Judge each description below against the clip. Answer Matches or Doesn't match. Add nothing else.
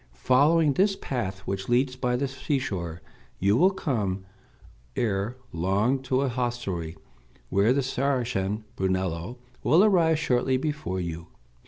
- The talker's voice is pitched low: Matches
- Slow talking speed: Matches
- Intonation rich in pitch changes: Matches